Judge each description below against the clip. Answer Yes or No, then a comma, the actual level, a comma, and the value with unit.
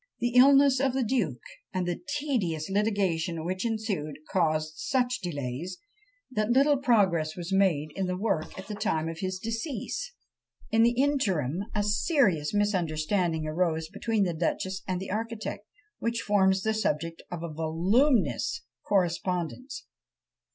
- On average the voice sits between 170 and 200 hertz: Yes, high, 190 Hz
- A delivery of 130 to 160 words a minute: Yes, average, 145 wpm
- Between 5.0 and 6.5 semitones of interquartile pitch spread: Yes, wide, 5.6 semitones